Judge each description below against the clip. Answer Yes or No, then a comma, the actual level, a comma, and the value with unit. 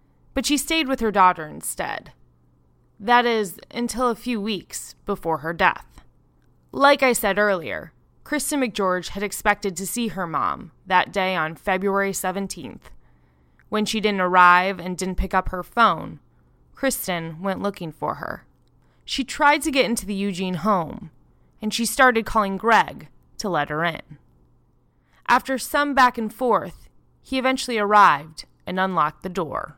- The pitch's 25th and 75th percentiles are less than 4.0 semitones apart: No, average, 4.8 semitones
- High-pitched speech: Yes, high, 200 Hz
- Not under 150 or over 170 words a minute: Yes, average, 155 wpm